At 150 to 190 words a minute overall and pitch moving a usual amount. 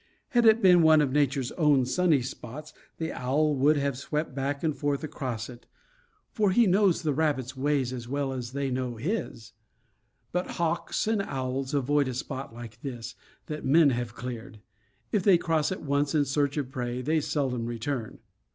Yes: average, 180 wpm; average, 3.5 semitones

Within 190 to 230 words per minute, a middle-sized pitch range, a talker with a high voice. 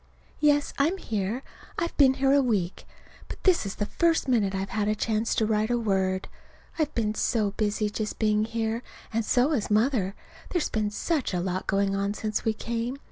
Yes: average, 195 wpm; average, 4.0 semitones; high, 220 Hz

